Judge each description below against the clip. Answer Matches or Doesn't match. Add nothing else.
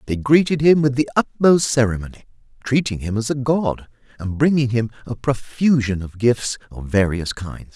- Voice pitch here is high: Doesn't match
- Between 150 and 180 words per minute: Matches